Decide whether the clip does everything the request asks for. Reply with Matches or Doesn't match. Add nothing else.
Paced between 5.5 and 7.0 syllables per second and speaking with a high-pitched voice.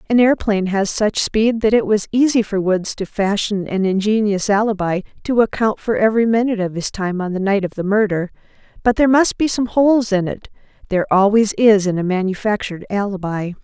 Matches